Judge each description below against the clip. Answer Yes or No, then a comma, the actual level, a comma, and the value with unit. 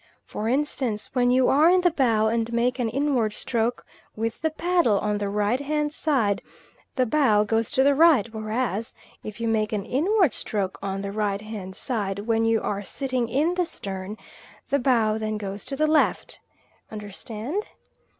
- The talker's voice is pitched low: No, high, 230 Hz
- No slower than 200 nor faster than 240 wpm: No, average, 180 wpm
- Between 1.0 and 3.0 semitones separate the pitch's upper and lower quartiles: No, average, 4.7 semitones